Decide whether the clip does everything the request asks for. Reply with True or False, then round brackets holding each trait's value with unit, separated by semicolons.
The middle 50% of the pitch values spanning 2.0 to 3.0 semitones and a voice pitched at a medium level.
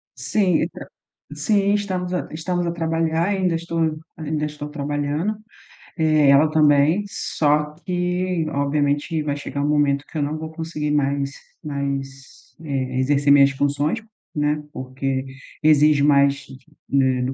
True (2.6 semitones; 150 Hz)